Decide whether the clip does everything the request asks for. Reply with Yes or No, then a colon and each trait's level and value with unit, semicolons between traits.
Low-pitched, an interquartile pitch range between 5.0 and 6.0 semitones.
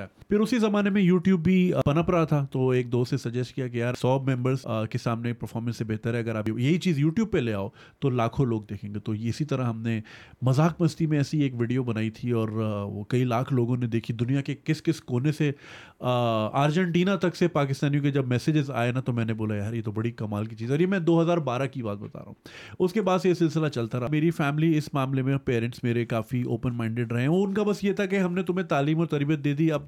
Yes: low, 130 Hz; wide, 5.4 semitones